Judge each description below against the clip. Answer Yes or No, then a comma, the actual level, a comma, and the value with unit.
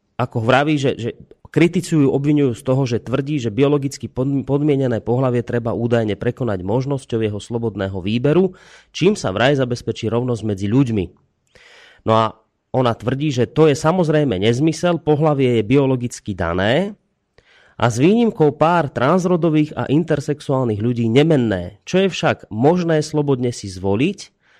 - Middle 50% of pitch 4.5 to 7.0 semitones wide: Yes, average, 4.8 semitones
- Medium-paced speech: Yes, average, 140 wpm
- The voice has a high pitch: No, low, 130 Hz